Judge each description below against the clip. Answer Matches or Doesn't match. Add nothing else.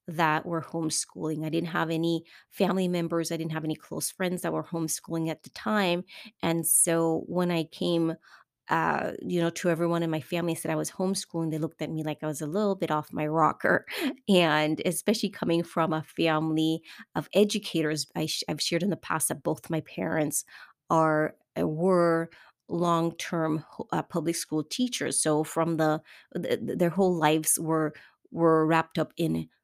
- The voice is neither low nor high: Matches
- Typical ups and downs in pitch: Doesn't match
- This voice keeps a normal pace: Matches